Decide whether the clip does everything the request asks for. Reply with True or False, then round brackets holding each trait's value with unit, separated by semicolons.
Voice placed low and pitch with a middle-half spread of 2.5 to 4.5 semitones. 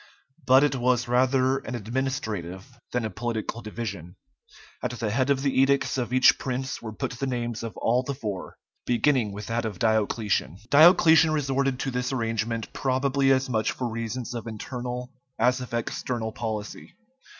True (125 Hz; 3.0 semitones)